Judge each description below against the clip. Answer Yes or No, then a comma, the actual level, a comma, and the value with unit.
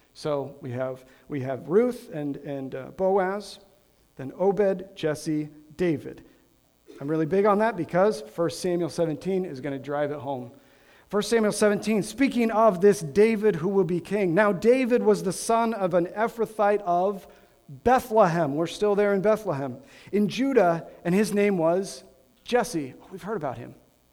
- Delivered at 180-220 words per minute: No, average, 165 wpm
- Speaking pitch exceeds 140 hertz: Yes, medium, 185 Hz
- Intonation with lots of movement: Yes, wide, 6.0 semitones